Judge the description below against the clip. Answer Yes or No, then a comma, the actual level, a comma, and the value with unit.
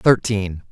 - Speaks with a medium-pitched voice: No, low, 105 Hz